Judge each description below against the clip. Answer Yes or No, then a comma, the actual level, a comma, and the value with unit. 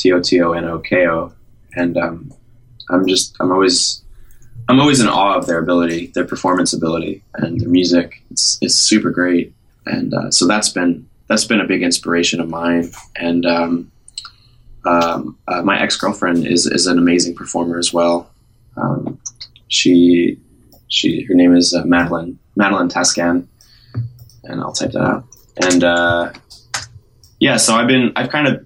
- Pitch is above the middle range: No, very low, 85 Hz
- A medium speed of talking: Yes, average, 170 wpm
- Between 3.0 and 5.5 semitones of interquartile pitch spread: No, narrow, 2.5 semitones